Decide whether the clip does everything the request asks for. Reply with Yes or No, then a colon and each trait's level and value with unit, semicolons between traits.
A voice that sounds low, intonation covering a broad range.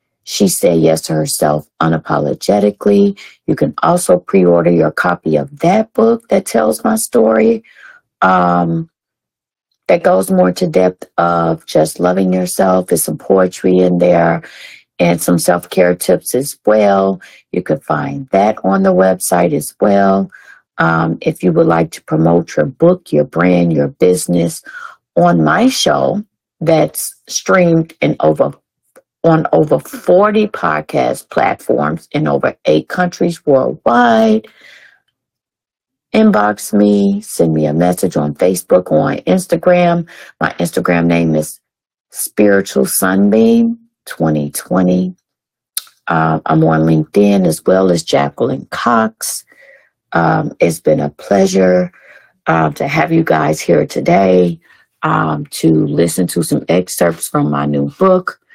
Yes: very low, 90 Hz; wide, 9.0 semitones